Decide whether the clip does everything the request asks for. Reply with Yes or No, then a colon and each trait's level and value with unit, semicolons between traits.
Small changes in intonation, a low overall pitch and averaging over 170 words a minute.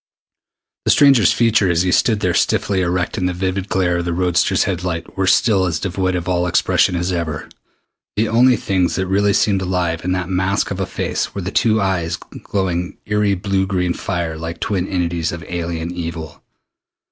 Yes: narrow, 2.1 semitones; very low, 90 Hz; average, 190 wpm